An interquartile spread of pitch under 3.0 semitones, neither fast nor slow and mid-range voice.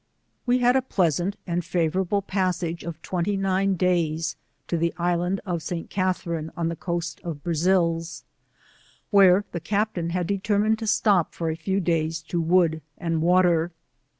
Yes: narrow, 2.4 semitones; average, 160 wpm; medium, 175 Hz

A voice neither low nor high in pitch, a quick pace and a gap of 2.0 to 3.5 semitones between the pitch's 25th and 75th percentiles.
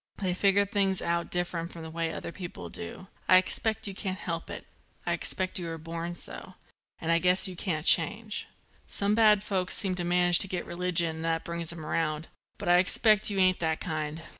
Yes: medium, 180 Hz; fast, 210 wpm; narrow, 2.6 semitones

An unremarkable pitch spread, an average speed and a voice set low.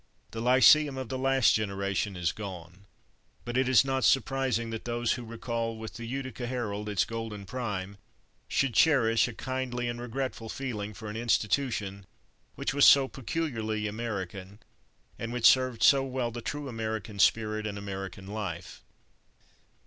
Yes: average, 3.9 semitones; average, 155 wpm; low, 115 Hz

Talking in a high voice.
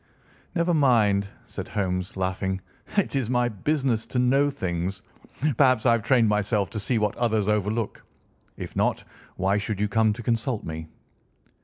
No: low, 110 Hz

